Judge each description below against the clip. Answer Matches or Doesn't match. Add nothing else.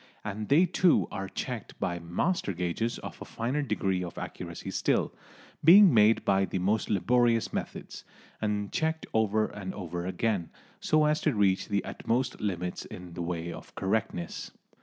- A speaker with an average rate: Matches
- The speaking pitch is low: Matches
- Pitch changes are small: Doesn't match